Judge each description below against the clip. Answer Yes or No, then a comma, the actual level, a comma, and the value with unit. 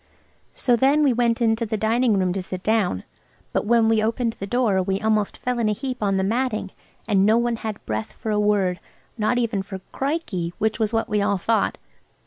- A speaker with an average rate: No, fast, 210 wpm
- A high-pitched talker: Yes, high, 220 Hz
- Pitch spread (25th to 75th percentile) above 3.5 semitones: No, average, 3.1 semitones